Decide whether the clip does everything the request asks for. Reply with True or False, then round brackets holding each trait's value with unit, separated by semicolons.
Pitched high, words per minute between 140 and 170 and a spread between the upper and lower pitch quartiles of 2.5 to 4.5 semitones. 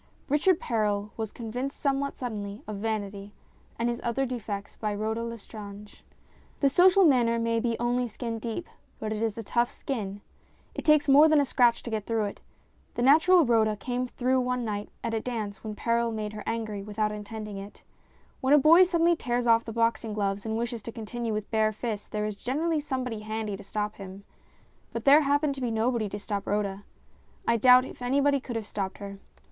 False (230 Hz; 200 wpm; 3.1 semitones)